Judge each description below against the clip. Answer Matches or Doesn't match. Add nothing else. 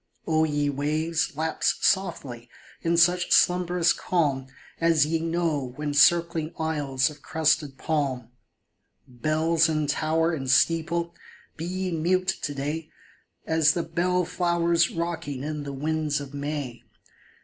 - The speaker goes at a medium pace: Doesn't match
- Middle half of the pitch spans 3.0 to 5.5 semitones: Doesn't match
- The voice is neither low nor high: Matches